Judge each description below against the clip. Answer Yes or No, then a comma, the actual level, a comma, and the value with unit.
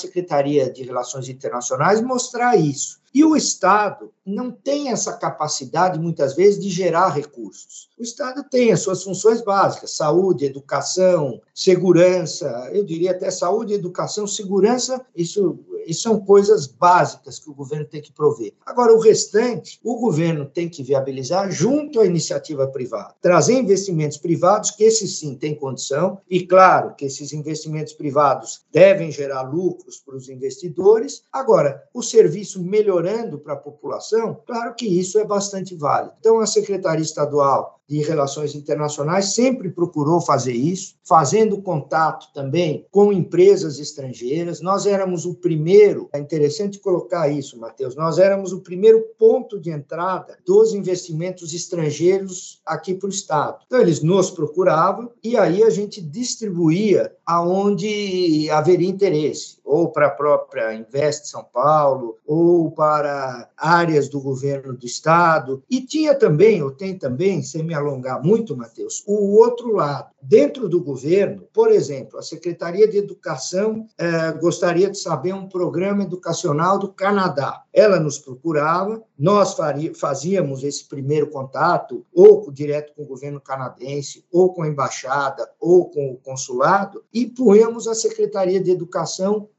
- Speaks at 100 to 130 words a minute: No, average, 145 wpm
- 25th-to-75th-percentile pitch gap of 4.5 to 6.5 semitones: Yes, wide, 5.4 semitones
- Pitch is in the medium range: Yes, medium, 180 Hz